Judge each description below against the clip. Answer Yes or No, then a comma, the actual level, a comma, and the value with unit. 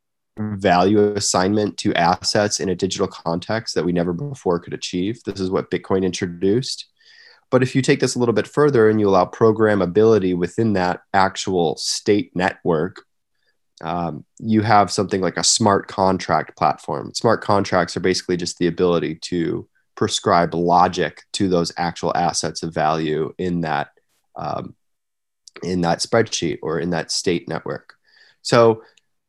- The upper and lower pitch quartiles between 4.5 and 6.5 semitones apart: No, average, 3.7 semitones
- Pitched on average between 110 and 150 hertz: No, very low, 95 Hz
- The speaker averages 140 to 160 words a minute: Yes, average, 150 wpm